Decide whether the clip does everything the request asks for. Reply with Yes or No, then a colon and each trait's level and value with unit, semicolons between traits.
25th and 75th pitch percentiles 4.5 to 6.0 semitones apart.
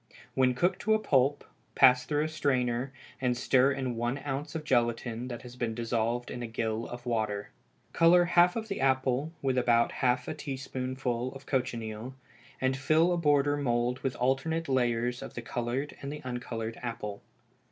No: average, 2.7 semitones